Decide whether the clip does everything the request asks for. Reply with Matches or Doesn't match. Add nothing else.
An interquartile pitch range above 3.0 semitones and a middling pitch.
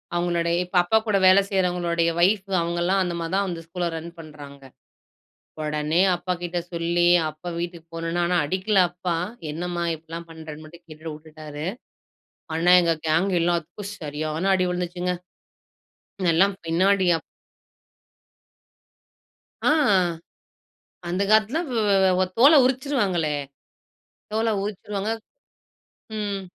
Doesn't match